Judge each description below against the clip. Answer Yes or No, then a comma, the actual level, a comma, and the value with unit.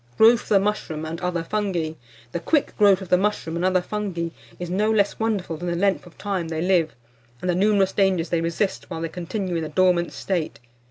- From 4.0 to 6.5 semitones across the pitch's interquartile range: No, average, 3.1 semitones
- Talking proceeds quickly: Yes, fast, 220 wpm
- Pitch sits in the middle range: Yes, medium, 180 Hz